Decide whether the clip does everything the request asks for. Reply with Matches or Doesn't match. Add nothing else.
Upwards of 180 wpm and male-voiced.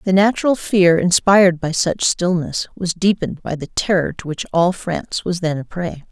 Doesn't match